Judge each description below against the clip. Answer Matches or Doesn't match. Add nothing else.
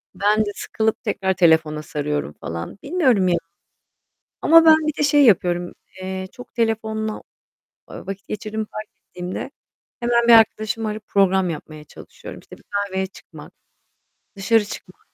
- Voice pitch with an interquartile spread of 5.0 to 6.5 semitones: Doesn't match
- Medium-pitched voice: Doesn't match